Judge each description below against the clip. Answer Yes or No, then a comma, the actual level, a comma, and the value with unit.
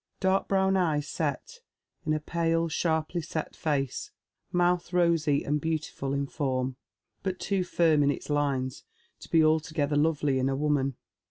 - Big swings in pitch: No, average, 3.0 semitones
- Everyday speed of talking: Yes, average, 160 wpm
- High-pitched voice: No, medium, 155 Hz